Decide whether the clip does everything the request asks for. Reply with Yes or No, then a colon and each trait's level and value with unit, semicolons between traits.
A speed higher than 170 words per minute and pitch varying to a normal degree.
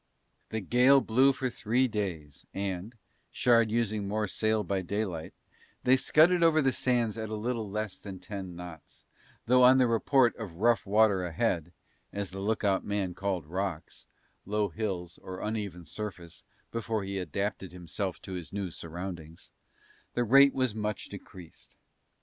No: average, 150 wpm; average, 3.9 semitones